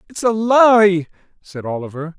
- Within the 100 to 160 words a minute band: Yes, slow, 135 wpm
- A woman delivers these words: No, male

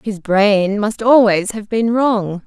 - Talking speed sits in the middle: Yes, average, 170 wpm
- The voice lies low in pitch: No, high, 210 Hz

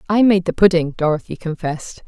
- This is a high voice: No, medium, 175 Hz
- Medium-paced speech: Yes, average, 175 wpm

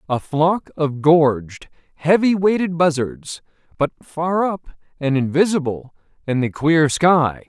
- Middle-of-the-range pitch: Yes, medium, 155 Hz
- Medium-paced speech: No, slow, 130 wpm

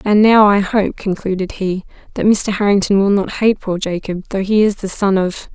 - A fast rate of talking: Yes, fast, 215 wpm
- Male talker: No, female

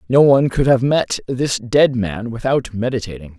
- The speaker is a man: Yes, male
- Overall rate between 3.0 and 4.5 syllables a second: No, 4.8 syllables/s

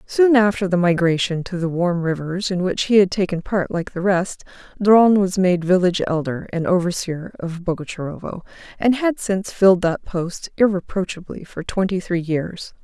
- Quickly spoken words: No, average, 175 wpm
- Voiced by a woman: Yes, female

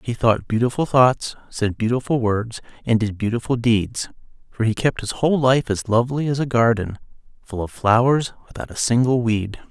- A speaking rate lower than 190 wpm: Yes, average, 180 wpm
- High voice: No, low, 120 Hz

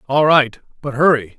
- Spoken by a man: Yes, male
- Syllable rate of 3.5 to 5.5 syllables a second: Yes, 5.0 syllables/s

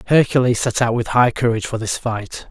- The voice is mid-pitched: No, low, 120 Hz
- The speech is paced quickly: Yes, fast, 215 wpm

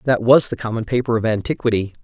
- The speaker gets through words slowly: No, fast, 205 wpm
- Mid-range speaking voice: No, low, 115 Hz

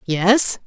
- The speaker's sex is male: No, female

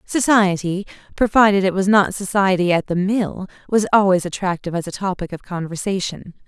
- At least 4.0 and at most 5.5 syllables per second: Yes, 5.4 syllables/s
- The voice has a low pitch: No, high, 190 Hz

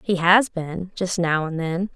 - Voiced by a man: No, female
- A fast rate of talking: No, average, 185 wpm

